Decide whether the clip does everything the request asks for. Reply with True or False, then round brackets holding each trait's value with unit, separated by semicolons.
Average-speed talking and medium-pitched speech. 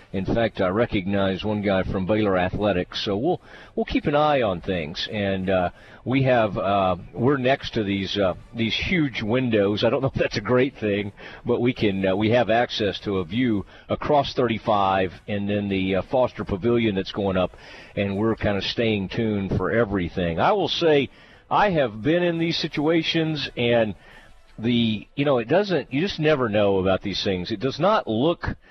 False (195 wpm; 110 Hz)